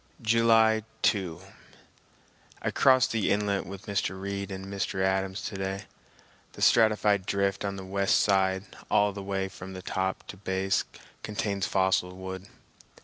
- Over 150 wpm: No, average, 145 wpm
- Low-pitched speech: Yes, low, 100 Hz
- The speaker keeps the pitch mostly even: Yes, narrow, 1.3 semitones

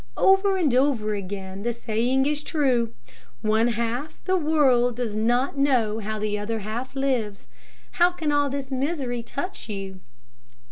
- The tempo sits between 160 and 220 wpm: No, average, 150 wpm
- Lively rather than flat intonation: No, average, 4.7 semitones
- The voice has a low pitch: No, high, 245 Hz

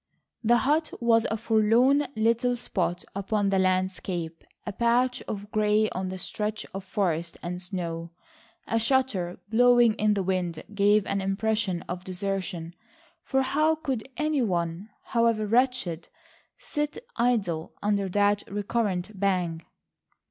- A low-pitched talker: No, high, 205 Hz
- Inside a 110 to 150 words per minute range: Yes, slow, 135 wpm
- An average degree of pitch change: Yes, average, 4.1 semitones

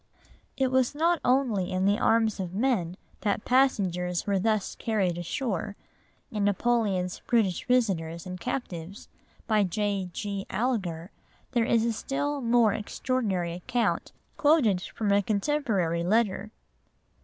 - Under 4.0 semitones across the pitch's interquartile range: No, average, 4.7 semitones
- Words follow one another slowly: Yes, slow, 130 wpm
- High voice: Yes, high, 210 Hz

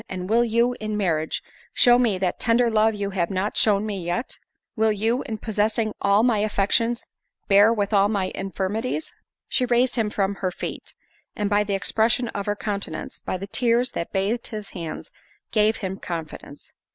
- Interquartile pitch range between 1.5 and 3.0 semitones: Yes, narrow, 2.6 semitones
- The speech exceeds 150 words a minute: Yes, average, 180 wpm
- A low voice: No, high, 210 Hz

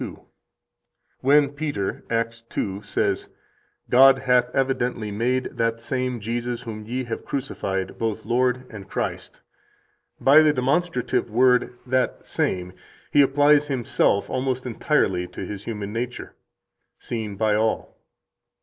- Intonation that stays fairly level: No, average, 3.3 semitones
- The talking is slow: Yes, slow, 125 wpm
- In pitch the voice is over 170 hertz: No, low, 125 Hz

